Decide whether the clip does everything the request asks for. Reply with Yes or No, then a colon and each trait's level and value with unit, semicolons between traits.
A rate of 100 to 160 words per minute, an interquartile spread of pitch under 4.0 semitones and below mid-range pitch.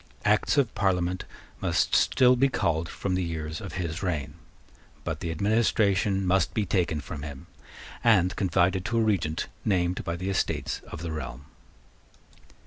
Yes: average, 155 wpm; average, 3.6 semitones; very low, 90 Hz